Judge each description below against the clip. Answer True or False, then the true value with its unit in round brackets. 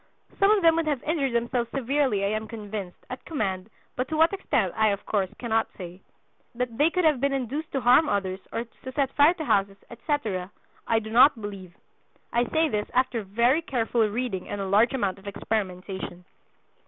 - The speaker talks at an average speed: True (195 wpm)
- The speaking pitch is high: True (230 Hz)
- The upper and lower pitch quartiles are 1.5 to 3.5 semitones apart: False (5.5 semitones)